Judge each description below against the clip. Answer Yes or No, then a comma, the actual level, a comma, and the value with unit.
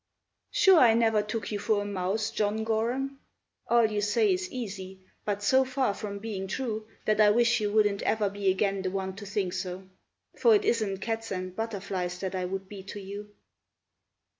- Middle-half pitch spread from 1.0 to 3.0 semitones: Yes, average, 2.7 semitones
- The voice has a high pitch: Yes, high, 210 Hz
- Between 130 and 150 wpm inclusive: No, average, 190 wpm